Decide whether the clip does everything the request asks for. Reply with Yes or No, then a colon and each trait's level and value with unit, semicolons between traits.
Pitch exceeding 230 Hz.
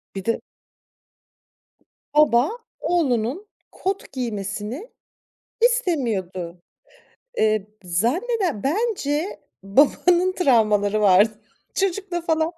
Yes: very high, 270 Hz